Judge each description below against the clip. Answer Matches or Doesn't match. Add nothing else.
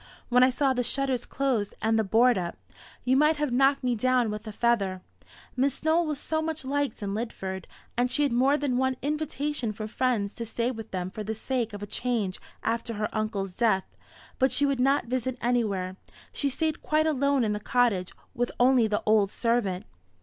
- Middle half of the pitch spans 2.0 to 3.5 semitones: Doesn't match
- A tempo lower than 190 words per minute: Doesn't match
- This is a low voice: Doesn't match